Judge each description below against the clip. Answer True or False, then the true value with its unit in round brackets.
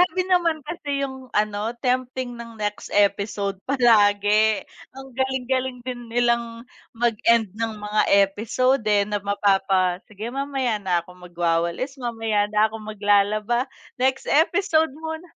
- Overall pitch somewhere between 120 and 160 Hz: False (230 Hz)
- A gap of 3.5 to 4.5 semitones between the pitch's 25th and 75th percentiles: True (4.1 semitones)